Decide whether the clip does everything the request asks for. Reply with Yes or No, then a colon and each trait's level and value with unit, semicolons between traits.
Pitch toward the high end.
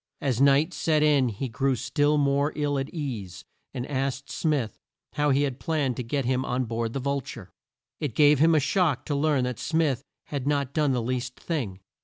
No: medium, 140 Hz